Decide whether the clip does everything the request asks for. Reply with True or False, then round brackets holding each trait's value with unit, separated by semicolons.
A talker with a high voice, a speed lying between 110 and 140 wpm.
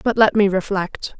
False (200 Hz; 200 wpm)